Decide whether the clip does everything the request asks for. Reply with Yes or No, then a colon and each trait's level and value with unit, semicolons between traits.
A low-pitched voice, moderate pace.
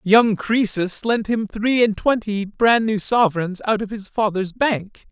No: high, 215 Hz; average, 175 wpm